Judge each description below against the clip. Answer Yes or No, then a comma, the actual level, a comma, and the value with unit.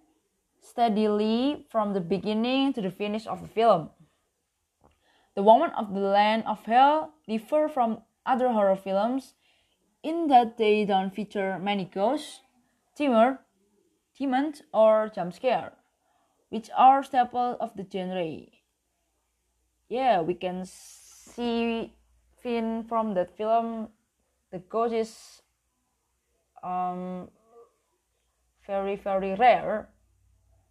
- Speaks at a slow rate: Yes, slow, 100 wpm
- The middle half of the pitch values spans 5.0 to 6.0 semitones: No, average, 3.8 semitones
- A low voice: No, high, 220 Hz